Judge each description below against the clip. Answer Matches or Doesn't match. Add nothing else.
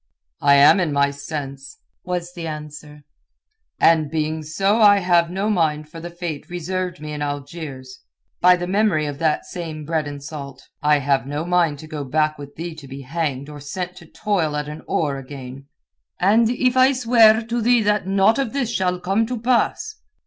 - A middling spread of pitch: Matches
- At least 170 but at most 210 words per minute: Matches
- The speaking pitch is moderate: Matches